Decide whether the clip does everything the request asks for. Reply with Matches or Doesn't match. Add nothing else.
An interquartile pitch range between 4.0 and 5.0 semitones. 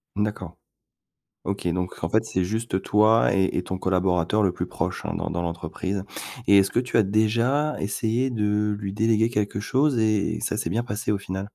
Doesn't match